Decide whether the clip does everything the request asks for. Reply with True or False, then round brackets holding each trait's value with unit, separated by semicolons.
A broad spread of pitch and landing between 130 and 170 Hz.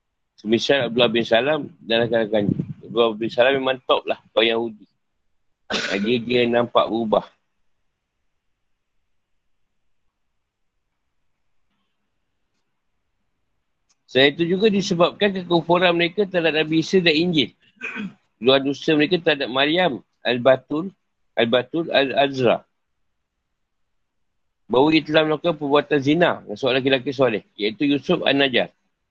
True (6.1 semitones; 140 Hz)